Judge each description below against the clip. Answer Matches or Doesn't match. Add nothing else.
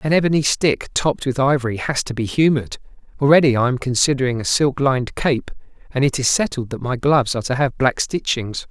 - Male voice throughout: Matches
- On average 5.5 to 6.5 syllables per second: Matches